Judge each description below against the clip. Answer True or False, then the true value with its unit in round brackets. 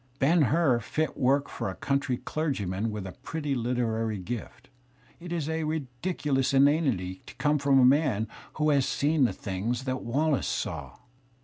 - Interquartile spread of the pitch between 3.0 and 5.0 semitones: True (4.3 semitones)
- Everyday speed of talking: True (155 wpm)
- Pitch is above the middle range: False (135 Hz)